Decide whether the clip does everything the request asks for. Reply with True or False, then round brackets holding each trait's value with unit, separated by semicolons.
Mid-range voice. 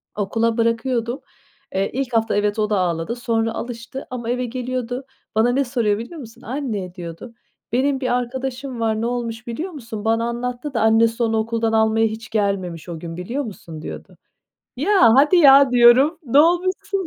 False (235 Hz)